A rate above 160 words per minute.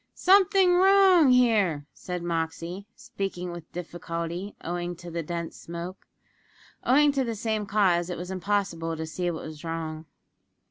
No: average, 145 wpm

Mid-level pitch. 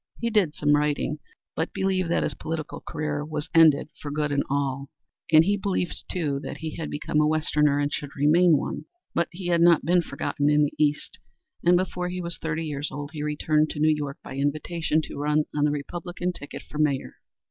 Yes: medium, 150 Hz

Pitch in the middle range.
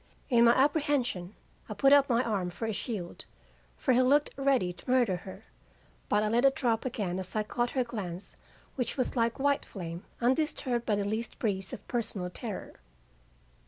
No: high, 235 Hz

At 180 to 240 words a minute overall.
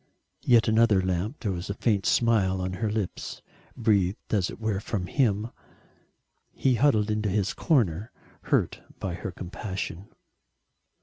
No: average, 140 wpm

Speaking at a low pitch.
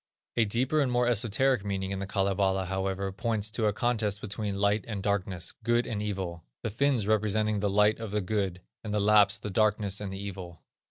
Yes: low, 105 Hz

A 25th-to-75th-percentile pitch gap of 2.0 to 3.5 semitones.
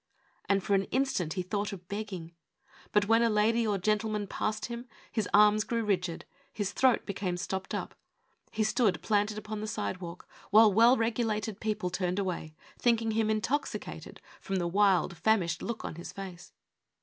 Yes: average, 2.8 semitones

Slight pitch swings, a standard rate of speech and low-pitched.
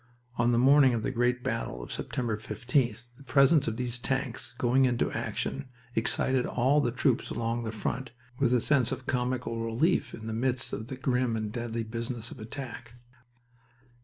Yes: narrow, 2.3 semitones; average, 180 wpm; low, 120 Hz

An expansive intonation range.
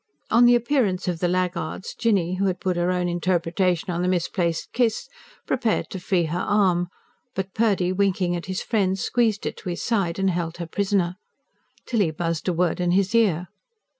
No: narrow, 2.4 semitones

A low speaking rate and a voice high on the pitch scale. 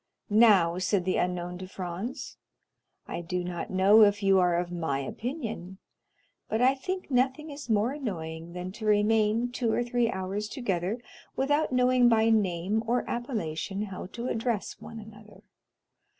No: average, 155 wpm; high, 210 Hz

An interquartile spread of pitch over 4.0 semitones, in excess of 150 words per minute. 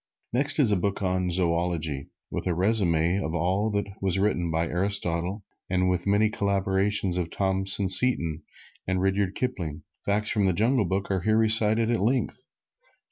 No: average, 3.0 semitones; average, 165 wpm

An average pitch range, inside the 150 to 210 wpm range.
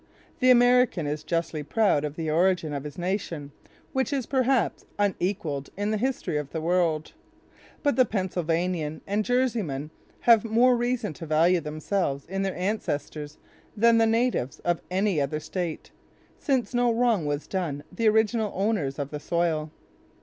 No: wide, 6.7 semitones; average, 155 wpm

